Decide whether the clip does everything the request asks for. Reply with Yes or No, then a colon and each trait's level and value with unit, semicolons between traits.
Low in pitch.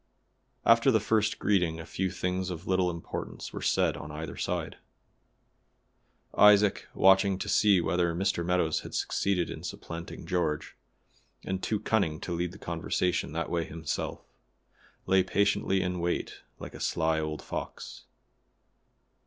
Yes: very low, 90 Hz